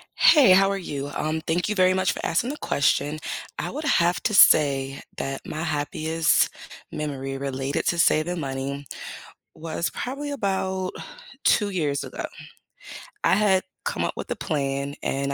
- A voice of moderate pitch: Yes, medium, 160 Hz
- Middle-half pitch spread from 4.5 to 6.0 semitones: Yes, average, 5.2 semitones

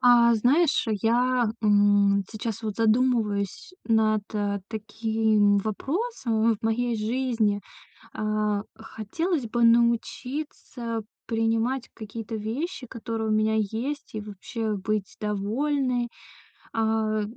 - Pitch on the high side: Yes, high, 225 Hz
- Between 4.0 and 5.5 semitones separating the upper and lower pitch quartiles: No, narrow, 2.4 semitones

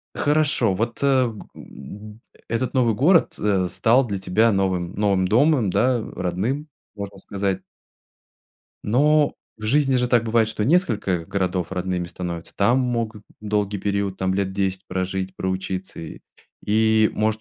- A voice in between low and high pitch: No, low, 105 Hz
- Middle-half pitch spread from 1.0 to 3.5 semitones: No, average, 3.9 semitones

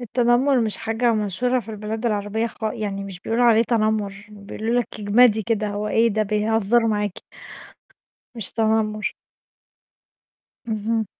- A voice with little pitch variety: Yes, narrow, 1.8 semitones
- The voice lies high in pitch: Yes, high, 220 Hz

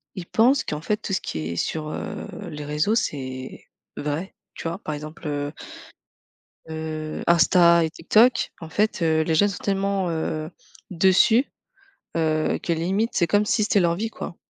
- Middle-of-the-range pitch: Yes, medium, 170 Hz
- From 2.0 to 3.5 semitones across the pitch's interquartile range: No, average, 4.3 semitones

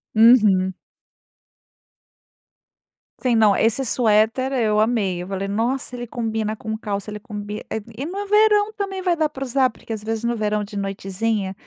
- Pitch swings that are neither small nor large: Yes, average, 3.7 semitones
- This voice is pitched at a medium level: No, high, 225 Hz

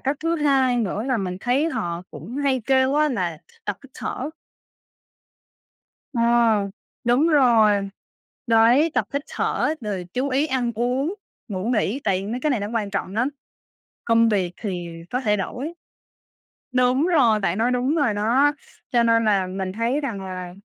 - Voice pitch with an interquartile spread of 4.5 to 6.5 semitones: Yes, average, 4.8 semitones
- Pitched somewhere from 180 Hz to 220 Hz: No, high, 235 Hz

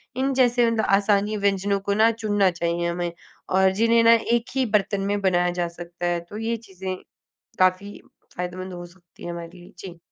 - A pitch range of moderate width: Yes, average, 3.6 semitones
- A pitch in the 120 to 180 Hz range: No, high, 190 Hz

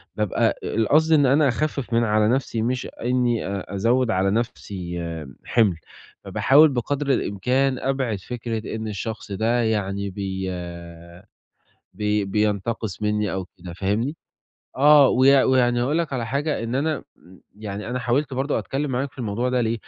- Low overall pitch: Yes, low, 115 Hz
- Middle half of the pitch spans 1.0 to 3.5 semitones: No, average, 4.1 semitones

